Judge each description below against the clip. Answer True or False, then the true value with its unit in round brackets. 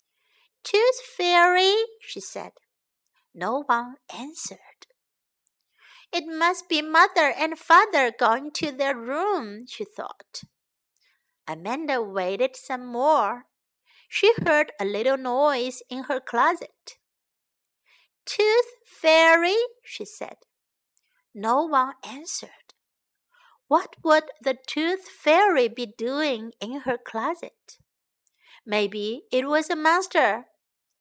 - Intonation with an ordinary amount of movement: False (6.6 semitones)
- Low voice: False (300 Hz)